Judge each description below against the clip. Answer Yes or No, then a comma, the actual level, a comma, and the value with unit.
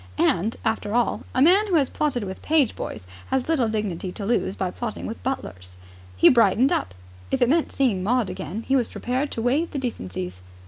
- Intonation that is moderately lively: No, wide, 6.0 semitones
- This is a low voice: No, high, 230 Hz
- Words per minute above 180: Yes, average, 200 wpm